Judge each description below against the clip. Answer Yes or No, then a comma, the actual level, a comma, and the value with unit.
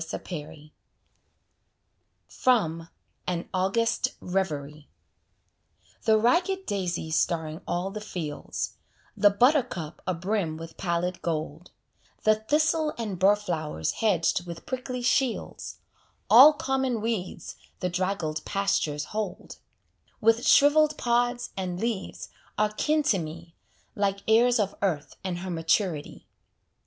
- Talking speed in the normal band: No, slow, 110 wpm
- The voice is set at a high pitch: Yes, high, 195 Hz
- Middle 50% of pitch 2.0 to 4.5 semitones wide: No, wide, 5.6 semitones